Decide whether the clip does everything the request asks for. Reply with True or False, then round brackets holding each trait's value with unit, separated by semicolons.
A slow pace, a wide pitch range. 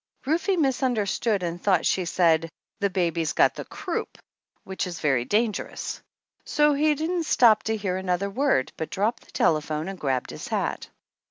False (165 wpm; 6.9 semitones)